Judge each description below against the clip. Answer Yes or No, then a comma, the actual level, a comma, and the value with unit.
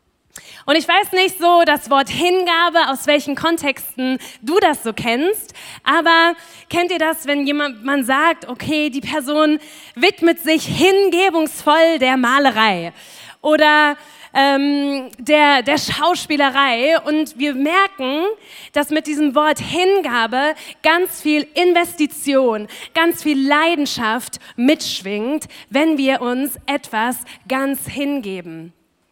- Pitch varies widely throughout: No, average, 3.4 semitones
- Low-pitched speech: No, very high, 295 Hz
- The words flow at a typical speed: No, slow, 115 wpm